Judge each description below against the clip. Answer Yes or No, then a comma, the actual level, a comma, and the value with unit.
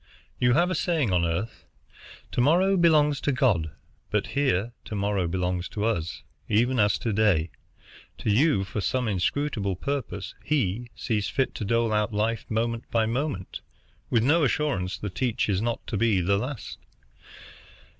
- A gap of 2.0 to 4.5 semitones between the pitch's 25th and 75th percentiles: No, average, 5.1 semitones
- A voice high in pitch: No, low, 115 Hz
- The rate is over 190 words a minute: No, average, 165 wpm